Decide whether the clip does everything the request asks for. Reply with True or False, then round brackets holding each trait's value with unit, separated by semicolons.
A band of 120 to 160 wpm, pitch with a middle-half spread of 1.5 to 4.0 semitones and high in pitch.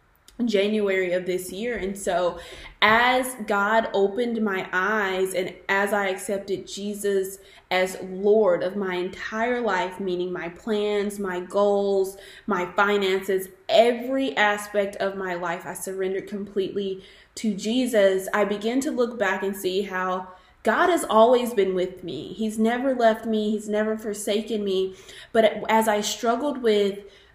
True (145 wpm; 2.4 semitones; 200 Hz)